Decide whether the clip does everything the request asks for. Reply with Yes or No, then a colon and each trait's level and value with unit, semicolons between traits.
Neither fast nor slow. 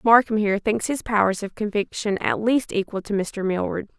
Yes: average, 195 wpm